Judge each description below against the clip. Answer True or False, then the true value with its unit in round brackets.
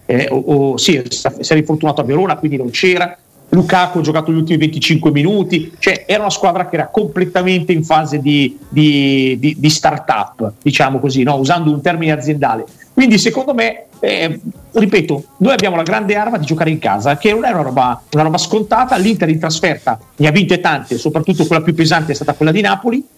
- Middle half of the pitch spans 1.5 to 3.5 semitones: False (4.3 semitones)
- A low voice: False (160 Hz)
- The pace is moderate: False (200 wpm)